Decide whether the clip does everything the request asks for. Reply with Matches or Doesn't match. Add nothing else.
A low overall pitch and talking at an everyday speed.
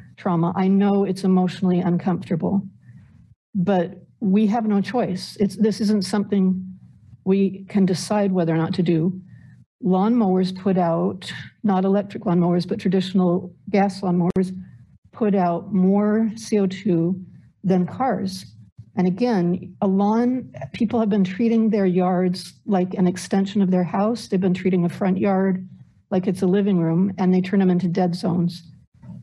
Doesn't match